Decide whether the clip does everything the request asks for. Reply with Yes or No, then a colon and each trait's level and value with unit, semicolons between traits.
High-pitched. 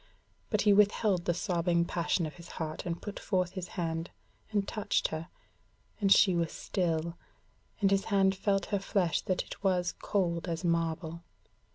No: medium, 180 Hz